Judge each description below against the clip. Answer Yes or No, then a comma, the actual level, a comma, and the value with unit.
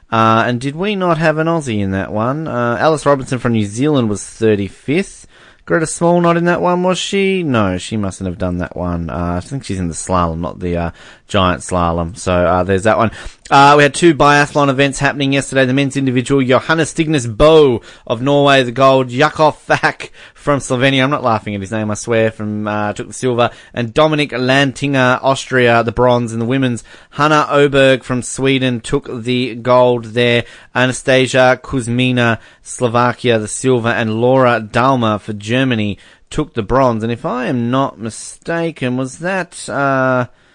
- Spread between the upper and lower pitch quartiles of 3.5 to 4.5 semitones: Yes, average, 4.1 semitones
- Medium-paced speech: Yes, average, 185 wpm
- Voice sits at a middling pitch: No, low, 125 Hz